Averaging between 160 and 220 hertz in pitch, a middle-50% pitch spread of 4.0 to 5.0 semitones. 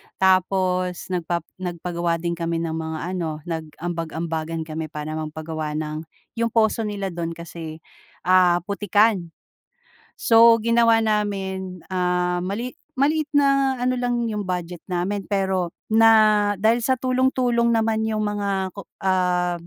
Yes: medium, 185 Hz; average, 4.5 semitones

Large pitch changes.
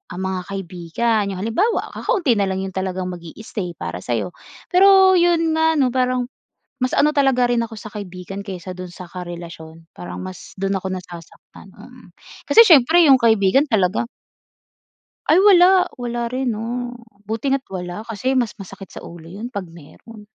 Yes: wide, 6.1 semitones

